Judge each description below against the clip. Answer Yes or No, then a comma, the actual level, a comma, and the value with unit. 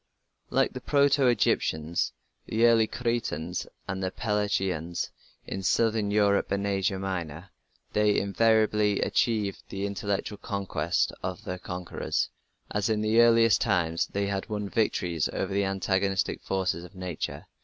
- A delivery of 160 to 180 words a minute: No, slow, 135 wpm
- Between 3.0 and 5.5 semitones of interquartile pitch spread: No, narrow, 2.6 semitones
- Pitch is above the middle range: No, low, 100 Hz